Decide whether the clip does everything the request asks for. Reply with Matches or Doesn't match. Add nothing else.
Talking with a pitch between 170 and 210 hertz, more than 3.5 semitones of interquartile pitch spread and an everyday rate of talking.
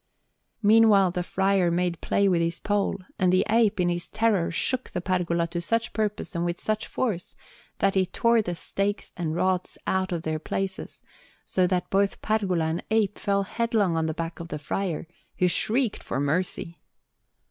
Doesn't match